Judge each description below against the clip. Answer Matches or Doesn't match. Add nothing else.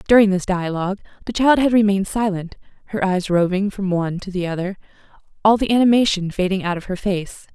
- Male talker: Doesn't match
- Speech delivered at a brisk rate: Doesn't match